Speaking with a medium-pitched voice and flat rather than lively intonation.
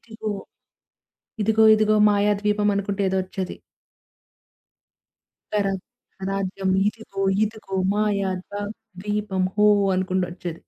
No: high, 205 Hz; narrow, 1.8 semitones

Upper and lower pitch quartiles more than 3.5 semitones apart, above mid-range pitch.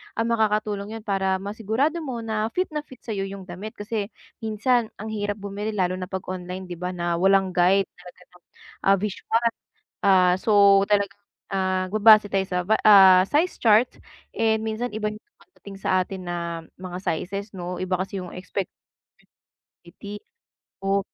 No: average, 2.8 semitones; high, 200 Hz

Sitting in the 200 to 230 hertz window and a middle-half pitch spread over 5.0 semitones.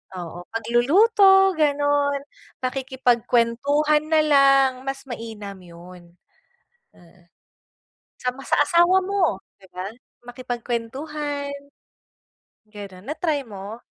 No: very high, 260 Hz; wide, 5.5 semitones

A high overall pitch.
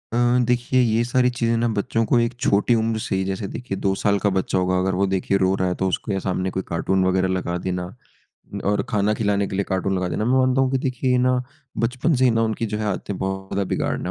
No: low, 105 Hz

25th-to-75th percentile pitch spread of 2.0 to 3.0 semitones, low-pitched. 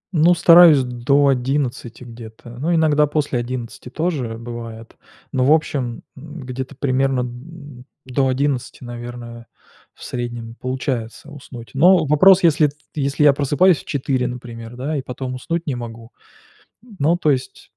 No: average, 3.5 semitones; low, 130 Hz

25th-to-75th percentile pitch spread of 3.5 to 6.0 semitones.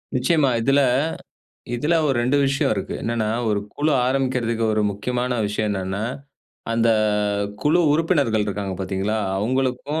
Yes: average, 4.5 semitones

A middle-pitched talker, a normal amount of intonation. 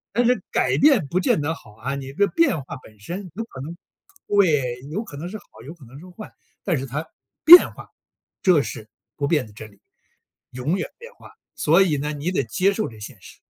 No: medium, 155 Hz; wide, 6.4 semitones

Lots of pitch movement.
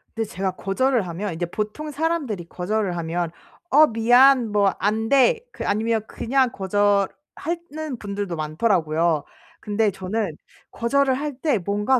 Yes: wide, 5.7 semitones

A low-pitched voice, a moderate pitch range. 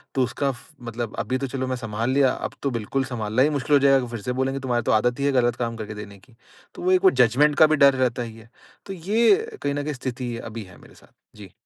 Yes: low, 125 Hz; average, 3.2 semitones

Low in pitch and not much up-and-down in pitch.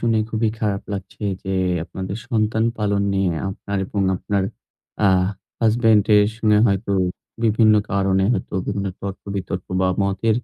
Yes: low, 100 Hz; narrow, 1.9 semitones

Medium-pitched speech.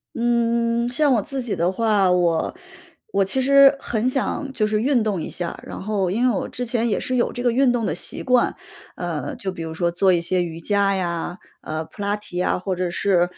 No: high, 205 Hz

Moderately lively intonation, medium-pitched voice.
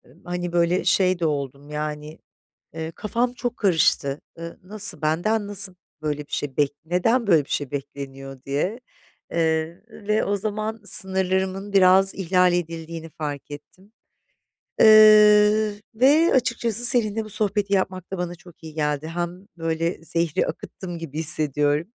Yes: average, 4.7 semitones; medium, 175 Hz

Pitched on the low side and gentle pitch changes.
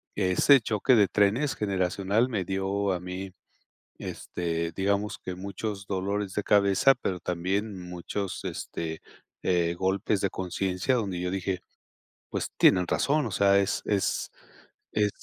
Yes: very low, 95 Hz; narrow, 2.1 semitones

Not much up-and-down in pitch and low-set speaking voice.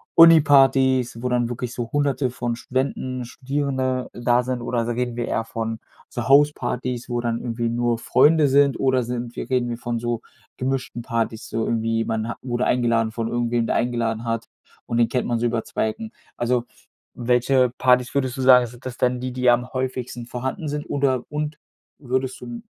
Yes: narrow, 1.7 semitones; low, 125 Hz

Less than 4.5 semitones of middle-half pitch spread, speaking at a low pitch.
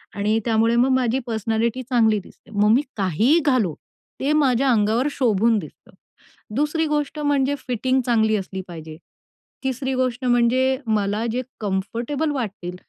No: average, 3.6 semitones; high, 235 Hz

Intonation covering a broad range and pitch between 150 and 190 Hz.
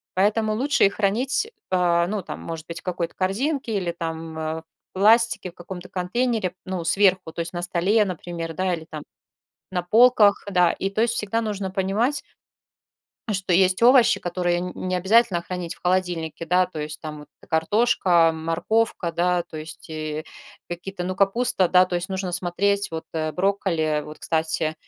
No: average, 3.1 semitones; medium, 185 Hz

